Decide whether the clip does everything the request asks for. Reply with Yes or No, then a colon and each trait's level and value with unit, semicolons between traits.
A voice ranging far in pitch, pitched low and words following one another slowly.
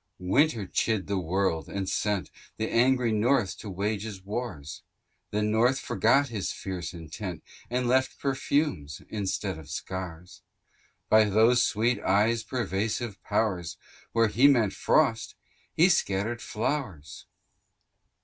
No: average, 4.3 semitones; low, 105 Hz; slow, 125 wpm